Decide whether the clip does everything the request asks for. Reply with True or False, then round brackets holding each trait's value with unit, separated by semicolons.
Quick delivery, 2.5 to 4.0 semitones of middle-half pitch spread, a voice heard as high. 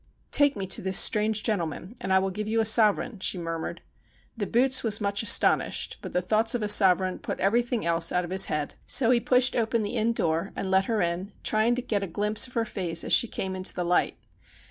True (240 wpm; 3.5 semitones; 205 Hz)